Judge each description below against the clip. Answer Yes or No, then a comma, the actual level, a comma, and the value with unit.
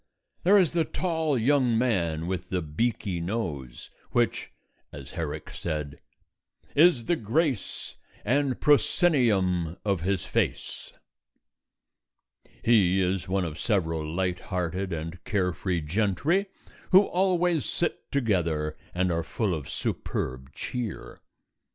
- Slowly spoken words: Yes, slow, 115 wpm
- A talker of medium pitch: No, very low, 95 Hz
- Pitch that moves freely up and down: Yes, wide, 8.2 semitones